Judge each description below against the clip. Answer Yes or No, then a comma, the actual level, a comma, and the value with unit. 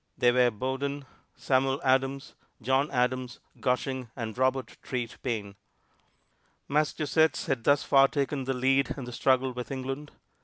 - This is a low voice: Yes, low, 130 Hz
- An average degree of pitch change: No, narrow, 1.7 semitones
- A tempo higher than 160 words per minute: No, average, 140 wpm